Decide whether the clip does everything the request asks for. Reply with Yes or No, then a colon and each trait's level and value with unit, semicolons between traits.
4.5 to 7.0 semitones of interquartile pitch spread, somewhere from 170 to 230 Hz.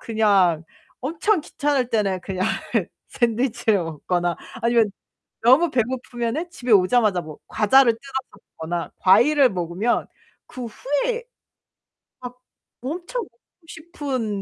No: wide, 5.6 semitones; high, 240 Hz